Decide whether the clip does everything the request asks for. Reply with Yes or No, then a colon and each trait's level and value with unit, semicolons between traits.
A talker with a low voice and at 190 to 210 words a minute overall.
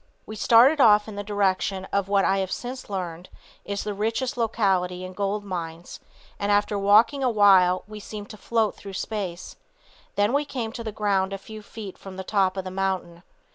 No: high, 205 Hz; average, 200 wpm